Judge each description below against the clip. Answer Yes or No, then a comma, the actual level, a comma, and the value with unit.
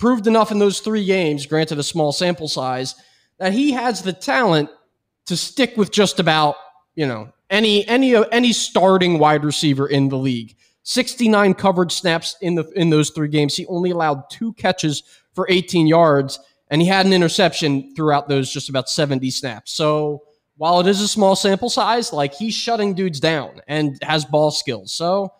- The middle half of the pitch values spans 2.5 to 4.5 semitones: No, average, 5.0 semitones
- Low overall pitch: No, medium, 165 Hz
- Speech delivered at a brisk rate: No, average, 185 wpm